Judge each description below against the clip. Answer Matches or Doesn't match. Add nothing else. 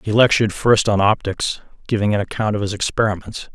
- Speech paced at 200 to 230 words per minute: Doesn't match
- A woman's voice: Doesn't match